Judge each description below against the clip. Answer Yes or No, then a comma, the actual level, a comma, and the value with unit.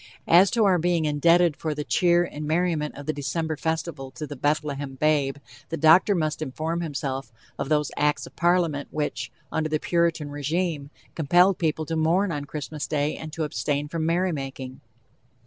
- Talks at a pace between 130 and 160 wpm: No, average, 175 wpm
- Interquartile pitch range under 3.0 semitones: Yes, narrow, 2.6 semitones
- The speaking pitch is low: No, medium, 155 Hz